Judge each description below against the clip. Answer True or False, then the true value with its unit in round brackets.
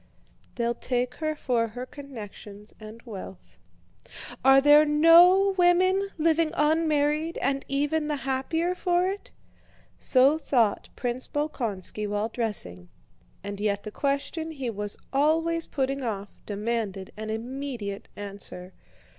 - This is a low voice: False (265 Hz)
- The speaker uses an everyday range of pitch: False (6.4 semitones)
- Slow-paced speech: True (120 wpm)